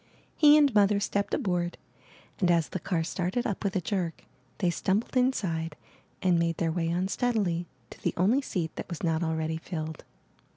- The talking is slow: No, average, 175 wpm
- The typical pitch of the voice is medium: Yes, medium, 180 Hz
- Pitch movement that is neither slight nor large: Yes, average, 3.5 semitones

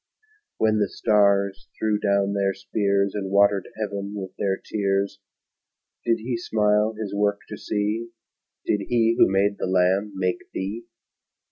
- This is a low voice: Yes, low, 100 Hz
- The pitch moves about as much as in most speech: No, narrow, 1.3 semitones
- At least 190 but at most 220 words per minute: No, average, 145 wpm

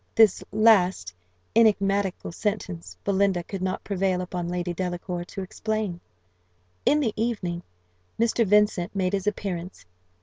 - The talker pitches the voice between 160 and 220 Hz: Yes, high, 190 Hz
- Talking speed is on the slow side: Yes, slow, 125 wpm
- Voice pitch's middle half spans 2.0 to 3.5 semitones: Yes, average, 2.9 semitones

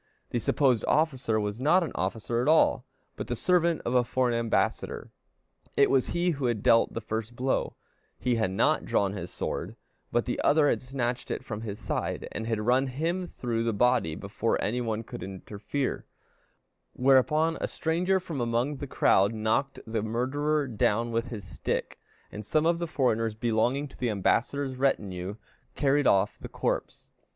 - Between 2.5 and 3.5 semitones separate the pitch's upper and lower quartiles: No, average, 4.3 semitones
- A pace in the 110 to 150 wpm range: No, average, 175 wpm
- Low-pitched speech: Yes, low, 120 Hz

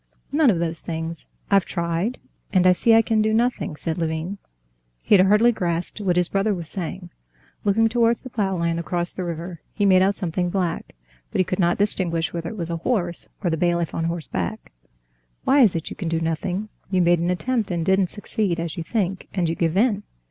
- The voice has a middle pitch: Yes, medium, 180 Hz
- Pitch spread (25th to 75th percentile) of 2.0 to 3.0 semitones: No, average, 3.4 semitones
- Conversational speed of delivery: No, fast, 215 wpm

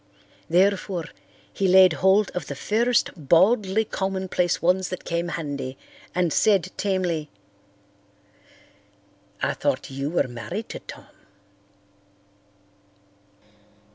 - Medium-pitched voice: Yes, medium, 180 Hz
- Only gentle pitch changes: No, average, 3.1 semitones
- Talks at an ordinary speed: No, slow, 100 wpm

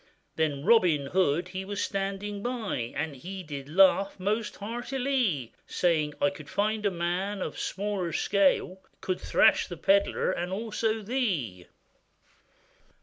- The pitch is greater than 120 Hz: Yes, high, 190 Hz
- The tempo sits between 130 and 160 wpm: Yes, average, 140 wpm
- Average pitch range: Yes, average, 3.6 semitones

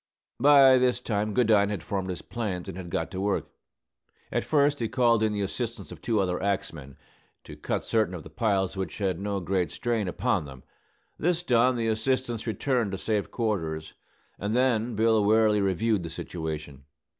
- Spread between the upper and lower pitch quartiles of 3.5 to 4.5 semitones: Yes, average, 4.1 semitones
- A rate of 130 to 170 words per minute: No, average, 180 wpm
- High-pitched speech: No, low, 105 Hz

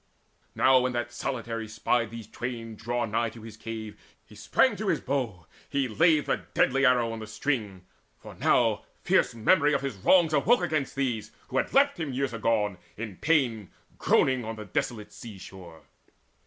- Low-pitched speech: Yes, low, 115 Hz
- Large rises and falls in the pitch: No, average, 3.9 semitones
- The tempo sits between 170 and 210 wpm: Yes, average, 175 wpm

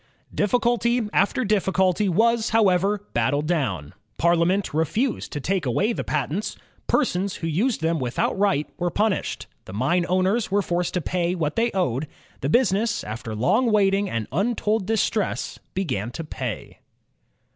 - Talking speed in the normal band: Yes, average, 150 wpm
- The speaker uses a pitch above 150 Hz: Yes, medium, 185 Hz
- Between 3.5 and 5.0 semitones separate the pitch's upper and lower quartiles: No, wide, 5.6 semitones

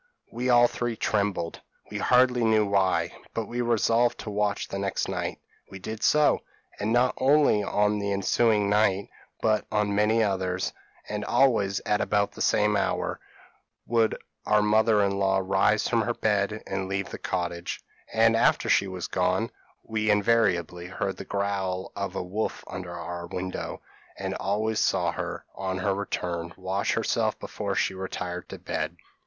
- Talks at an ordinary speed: Yes, average, 165 wpm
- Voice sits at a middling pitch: No, low, 100 Hz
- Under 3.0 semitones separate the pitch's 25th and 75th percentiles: Yes, narrow, 2.5 semitones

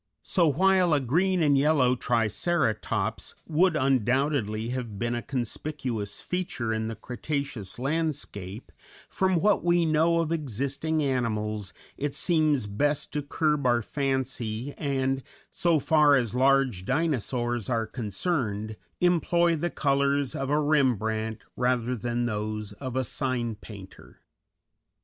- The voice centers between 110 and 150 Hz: Yes, low, 135 Hz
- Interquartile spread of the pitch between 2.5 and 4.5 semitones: No, average, 5.0 semitones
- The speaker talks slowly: Yes, slow, 125 wpm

